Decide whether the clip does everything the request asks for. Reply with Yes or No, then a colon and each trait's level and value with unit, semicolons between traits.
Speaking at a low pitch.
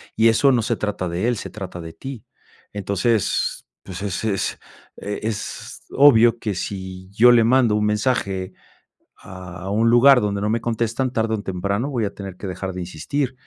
Yes: low, 105 Hz